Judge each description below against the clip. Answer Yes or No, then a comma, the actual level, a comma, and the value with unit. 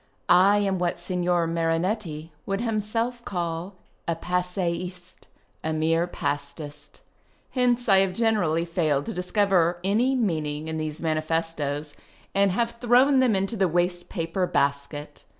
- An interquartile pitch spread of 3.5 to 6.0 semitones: Yes, average, 3.8 semitones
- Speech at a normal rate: No, slow, 130 wpm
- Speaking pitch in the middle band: Yes, medium, 175 Hz